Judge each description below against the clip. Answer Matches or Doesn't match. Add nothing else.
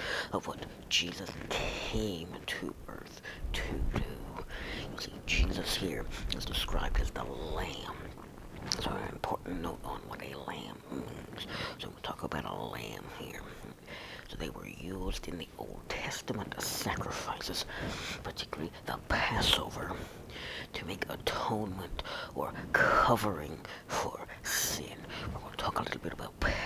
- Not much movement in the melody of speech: Matches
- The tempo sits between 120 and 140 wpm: Matches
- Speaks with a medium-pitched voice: Doesn't match